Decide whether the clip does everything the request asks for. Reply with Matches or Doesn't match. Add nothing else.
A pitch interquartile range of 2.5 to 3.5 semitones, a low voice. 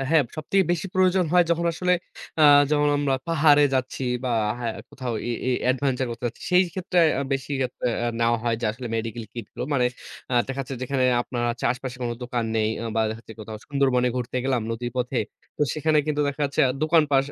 Doesn't match